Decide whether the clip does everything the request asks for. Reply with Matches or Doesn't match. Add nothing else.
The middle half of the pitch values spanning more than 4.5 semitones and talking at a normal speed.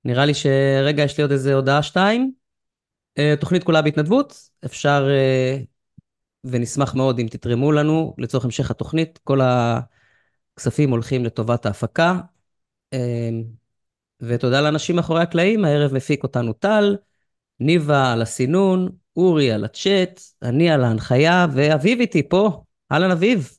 Matches